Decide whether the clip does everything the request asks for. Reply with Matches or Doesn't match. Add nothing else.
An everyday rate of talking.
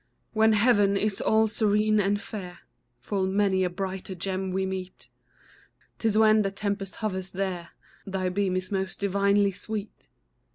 Matches